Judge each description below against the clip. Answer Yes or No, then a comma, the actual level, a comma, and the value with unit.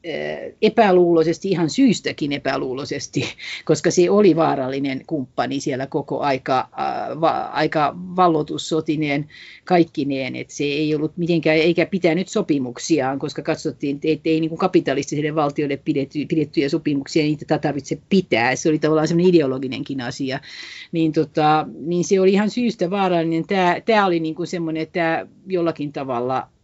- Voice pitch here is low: No, medium, 160 Hz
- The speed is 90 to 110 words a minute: No, average, 135 wpm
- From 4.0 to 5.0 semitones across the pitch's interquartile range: No, average, 3.1 semitones